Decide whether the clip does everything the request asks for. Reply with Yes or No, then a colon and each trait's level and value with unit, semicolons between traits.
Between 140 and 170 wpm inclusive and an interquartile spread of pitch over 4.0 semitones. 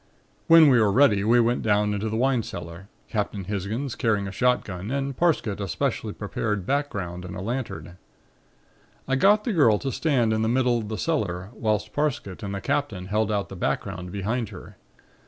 No: average, 190 wpm; average, 4.5 semitones